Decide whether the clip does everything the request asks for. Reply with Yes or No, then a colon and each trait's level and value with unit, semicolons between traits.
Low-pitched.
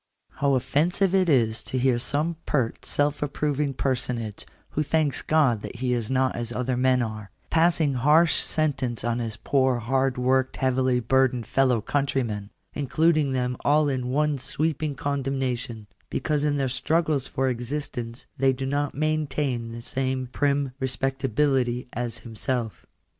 Yes: low, 130 Hz